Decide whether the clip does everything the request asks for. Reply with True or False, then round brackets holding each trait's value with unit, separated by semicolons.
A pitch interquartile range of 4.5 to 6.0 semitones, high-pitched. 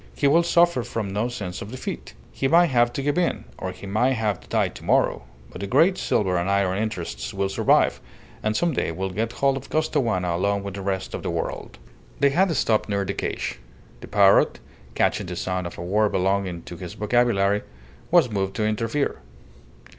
False (5.0 semitones; 105 Hz)